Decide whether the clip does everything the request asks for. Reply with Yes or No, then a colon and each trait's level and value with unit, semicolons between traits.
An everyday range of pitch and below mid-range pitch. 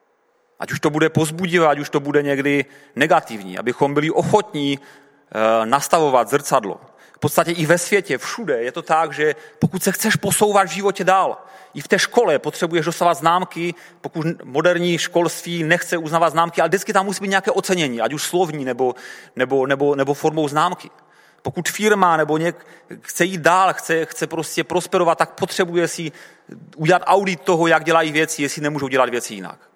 No: average, 3.6 semitones; medium, 165 Hz